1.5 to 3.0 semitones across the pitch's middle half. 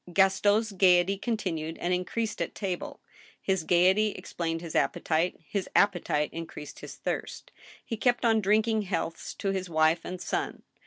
No: average, 3.8 semitones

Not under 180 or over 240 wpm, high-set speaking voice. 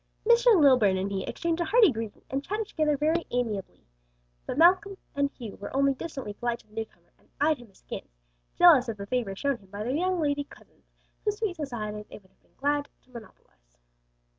Yes: fast, 205 wpm; very high, 270 Hz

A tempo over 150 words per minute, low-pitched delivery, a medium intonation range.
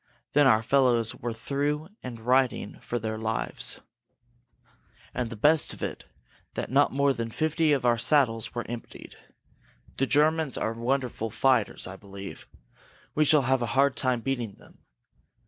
Yes: average, 160 wpm; low, 125 Hz; average, 3.7 semitones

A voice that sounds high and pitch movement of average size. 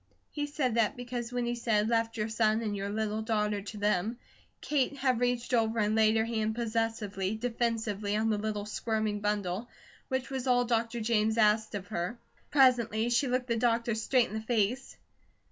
No: high, 225 Hz; narrow, 2.1 semitones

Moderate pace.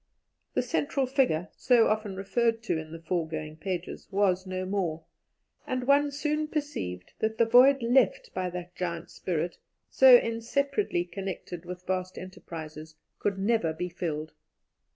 Yes: average, 145 wpm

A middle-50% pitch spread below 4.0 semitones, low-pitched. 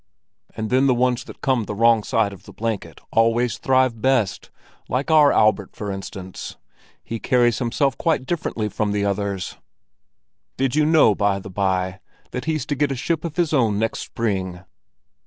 No: average, 4.7 semitones; low, 115 Hz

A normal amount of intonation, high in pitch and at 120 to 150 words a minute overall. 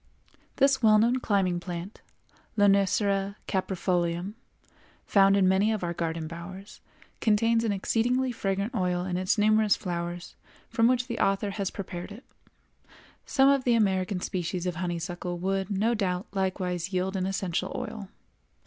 Yes: average, 3.0 semitones; high, 195 Hz; average, 145 wpm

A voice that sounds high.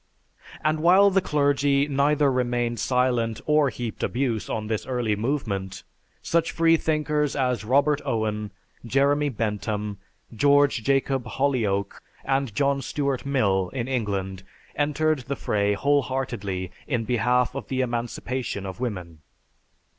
No: low, 125 Hz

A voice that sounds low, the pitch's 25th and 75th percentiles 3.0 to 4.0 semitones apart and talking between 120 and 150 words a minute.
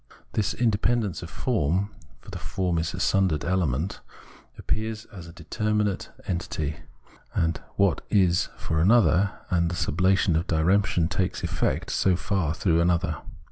Yes: very low, 90 Hz; average, 3.3 semitones; average, 140 wpm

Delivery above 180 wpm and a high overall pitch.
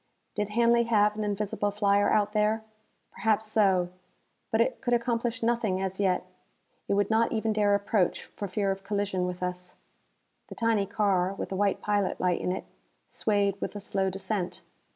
No: average, 175 wpm; high, 205 Hz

